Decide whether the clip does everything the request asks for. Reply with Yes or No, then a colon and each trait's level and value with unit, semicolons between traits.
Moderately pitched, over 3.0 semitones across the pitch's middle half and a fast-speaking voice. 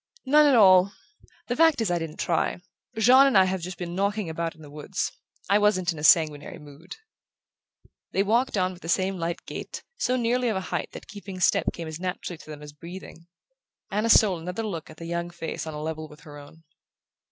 Yes: medium, 180 Hz; average, 4.3 semitones; fast, 220 wpm